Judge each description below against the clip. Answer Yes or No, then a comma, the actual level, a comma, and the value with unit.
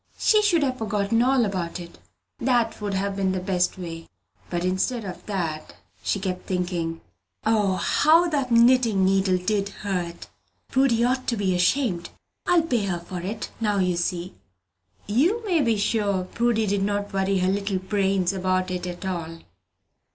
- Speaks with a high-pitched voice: Yes, high, 195 Hz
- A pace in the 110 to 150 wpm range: No, average, 165 wpm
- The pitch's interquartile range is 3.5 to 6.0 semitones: Yes, average, 4.1 semitones